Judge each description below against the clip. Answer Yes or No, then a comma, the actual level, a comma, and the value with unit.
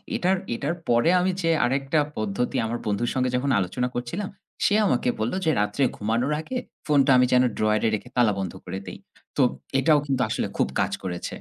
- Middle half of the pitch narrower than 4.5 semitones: No, average, 5.2 semitones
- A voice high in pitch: No, low, 125 Hz